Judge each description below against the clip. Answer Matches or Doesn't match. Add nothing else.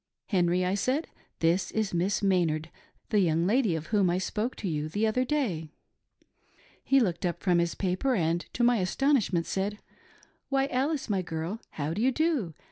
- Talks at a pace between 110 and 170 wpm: Doesn't match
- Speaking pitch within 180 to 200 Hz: Matches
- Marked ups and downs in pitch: Matches